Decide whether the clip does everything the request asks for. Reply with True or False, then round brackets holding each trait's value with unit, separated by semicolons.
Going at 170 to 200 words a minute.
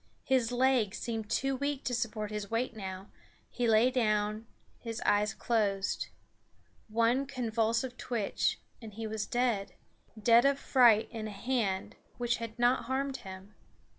False (145 wpm)